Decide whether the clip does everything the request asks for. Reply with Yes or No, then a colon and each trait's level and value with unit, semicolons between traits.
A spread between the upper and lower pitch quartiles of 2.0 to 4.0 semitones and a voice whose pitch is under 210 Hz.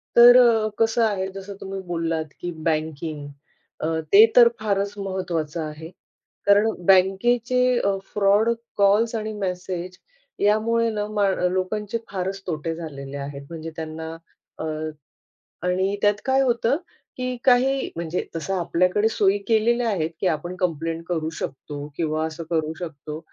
No: average, 4.9 semitones; high, 190 Hz